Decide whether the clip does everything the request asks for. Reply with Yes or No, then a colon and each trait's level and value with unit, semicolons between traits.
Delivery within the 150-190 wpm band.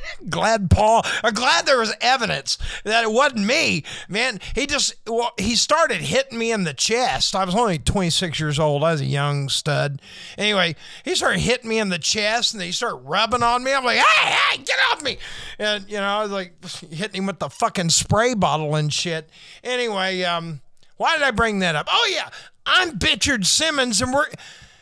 No: fast, 205 wpm